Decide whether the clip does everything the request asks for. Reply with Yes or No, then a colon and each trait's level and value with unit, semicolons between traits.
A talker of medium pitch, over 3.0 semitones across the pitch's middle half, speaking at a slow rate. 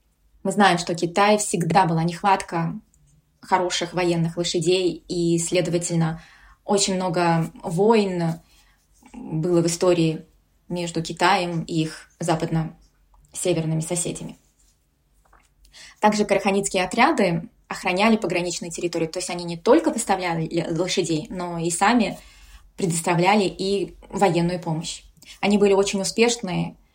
No: medium, 175 Hz; narrow, 2.6 semitones; slow, 105 wpm